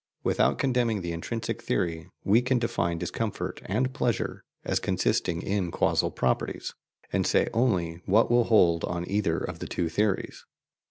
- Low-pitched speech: Yes, low, 100 Hz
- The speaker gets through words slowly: No, average, 155 wpm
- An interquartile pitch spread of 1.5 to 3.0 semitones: No, wide, 5.4 semitones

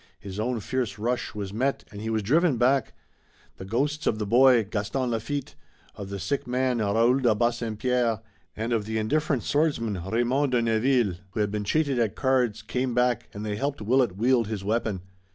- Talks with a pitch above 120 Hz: No, low, 115 Hz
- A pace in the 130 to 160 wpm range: No, average, 190 wpm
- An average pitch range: Yes, average, 3.4 semitones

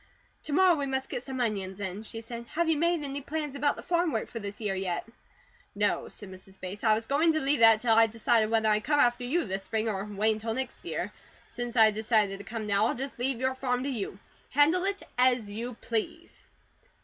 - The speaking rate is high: Yes, fast, 230 wpm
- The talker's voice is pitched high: Yes, high, 235 Hz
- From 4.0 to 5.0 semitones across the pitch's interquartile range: Yes, average, 4.7 semitones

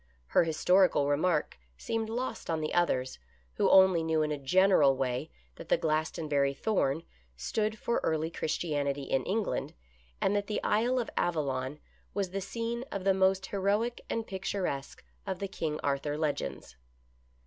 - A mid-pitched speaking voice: Yes, medium, 170 Hz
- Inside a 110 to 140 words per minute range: No, average, 160 wpm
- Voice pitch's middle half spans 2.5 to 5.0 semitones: No, wide, 5.5 semitones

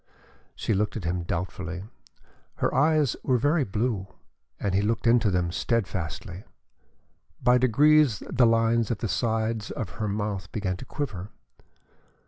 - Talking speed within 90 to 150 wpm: Yes, average, 140 wpm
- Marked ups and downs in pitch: No, average, 4.2 semitones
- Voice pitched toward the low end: Yes, low, 110 Hz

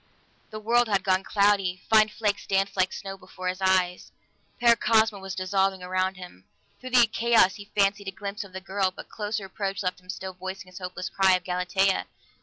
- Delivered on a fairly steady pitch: Yes, narrow, 1.8 semitones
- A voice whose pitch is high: Yes, high, 195 Hz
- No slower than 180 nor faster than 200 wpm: Yes, average, 195 wpm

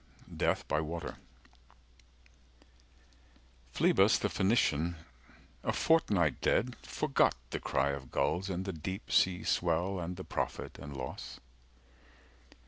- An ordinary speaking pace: No, slow, 115 wpm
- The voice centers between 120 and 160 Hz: No, very low, 85 Hz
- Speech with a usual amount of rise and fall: Yes, average, 4.1 semitones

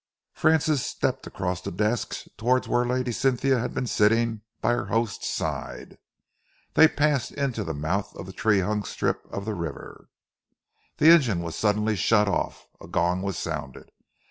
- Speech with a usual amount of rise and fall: Yes, average, 4.7 semitones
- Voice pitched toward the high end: No, low, 110 Hz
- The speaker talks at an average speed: Yes, average, 170 wpm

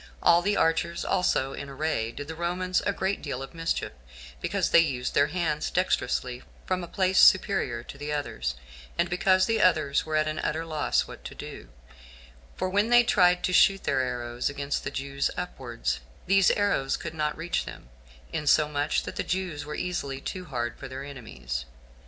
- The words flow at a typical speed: Yes, average, 185 wpm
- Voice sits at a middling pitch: Yes, medium, 155 Hz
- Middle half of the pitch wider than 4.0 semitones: Yes, average, 5.0 semitones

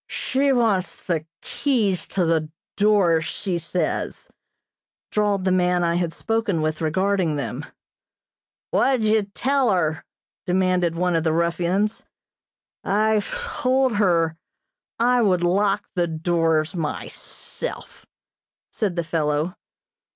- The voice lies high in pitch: No, medium, 180 Hz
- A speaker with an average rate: No, slow, 120 wpm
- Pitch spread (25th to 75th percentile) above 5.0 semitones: No, average, 4.2 semitones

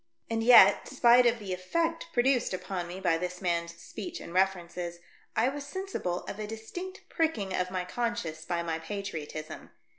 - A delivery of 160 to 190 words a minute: Yes, average, 175 wpm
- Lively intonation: Yes, wide, 5.7 semitones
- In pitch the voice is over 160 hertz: Yes, high, 190 Hz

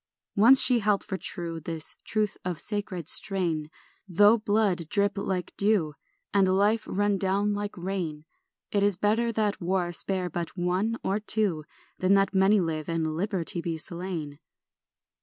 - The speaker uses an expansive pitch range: No, average, 3.2 semitones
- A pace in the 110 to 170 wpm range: Yes, average, 155 wpm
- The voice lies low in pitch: No, high, 190 Hz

